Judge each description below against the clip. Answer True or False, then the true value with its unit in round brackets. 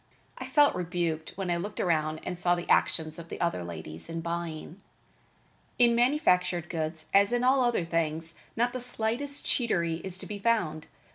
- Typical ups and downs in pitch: False (6.1 semitones)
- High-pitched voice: False (175 Hz)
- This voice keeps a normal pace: True (180 wpm)